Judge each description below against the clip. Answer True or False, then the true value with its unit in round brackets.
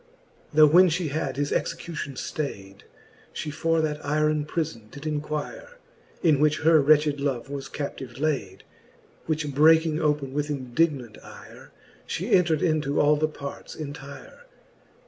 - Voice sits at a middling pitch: True (150 Hz)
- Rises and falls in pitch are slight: True (2.0 semitones)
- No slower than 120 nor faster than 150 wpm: True (145 wpm)